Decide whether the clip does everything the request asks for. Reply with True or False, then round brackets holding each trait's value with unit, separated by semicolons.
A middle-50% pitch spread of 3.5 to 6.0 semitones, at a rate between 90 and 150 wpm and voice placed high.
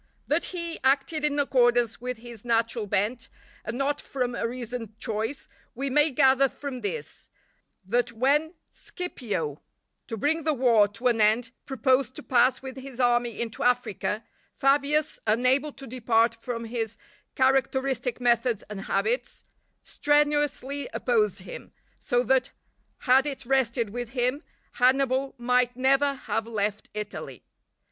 False (2.9 semitones; 140 wpm; 250 Hz)